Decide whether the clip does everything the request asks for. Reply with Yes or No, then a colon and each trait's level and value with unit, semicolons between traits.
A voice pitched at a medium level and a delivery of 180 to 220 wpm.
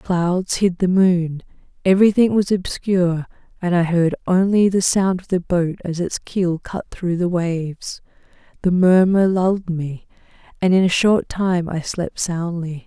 No: medium, 180 Hz; average, 165 wpm